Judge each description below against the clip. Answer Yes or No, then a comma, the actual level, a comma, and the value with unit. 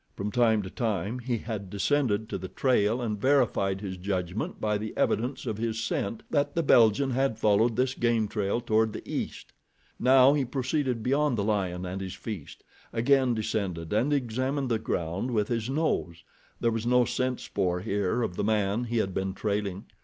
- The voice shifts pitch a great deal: No, average, 3.9 semitones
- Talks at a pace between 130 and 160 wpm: No, average, 185 wpm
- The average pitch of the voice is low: Yes, low, 110 Hz